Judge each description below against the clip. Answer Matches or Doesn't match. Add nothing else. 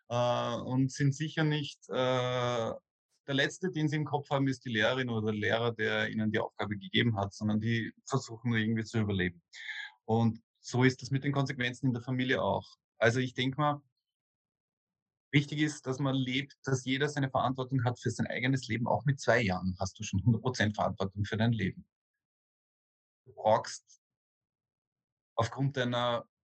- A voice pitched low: Matches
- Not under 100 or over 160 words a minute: Doesn't match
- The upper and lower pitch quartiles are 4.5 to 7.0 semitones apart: Doesn't match